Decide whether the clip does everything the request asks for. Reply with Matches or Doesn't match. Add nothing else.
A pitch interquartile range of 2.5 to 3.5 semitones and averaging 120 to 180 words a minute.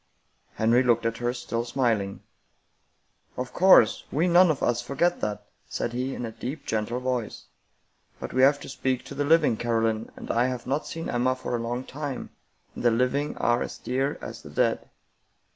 Doesn't match